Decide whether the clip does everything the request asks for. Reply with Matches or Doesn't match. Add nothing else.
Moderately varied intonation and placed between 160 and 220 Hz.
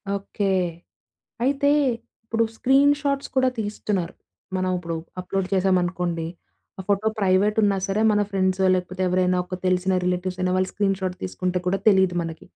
Doesn't match